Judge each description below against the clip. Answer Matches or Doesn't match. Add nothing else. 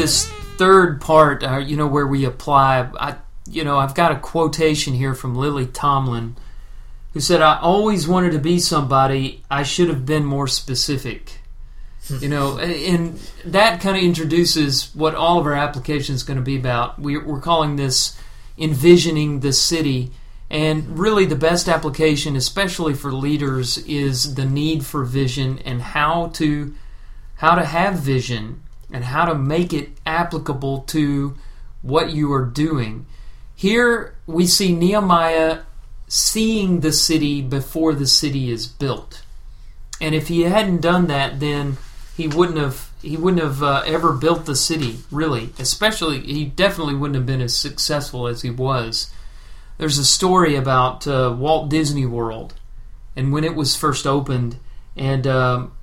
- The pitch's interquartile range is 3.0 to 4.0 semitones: Matches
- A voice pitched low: Doesn't match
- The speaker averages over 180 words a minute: Doesn't match